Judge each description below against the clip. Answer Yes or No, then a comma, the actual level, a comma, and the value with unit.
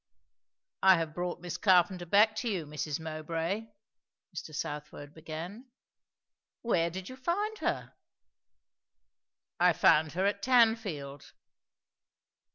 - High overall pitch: No, medium, 175 Hz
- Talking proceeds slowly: Yes, slow, 110 wpm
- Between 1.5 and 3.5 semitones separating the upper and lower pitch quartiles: No, wide, 5.4 semitones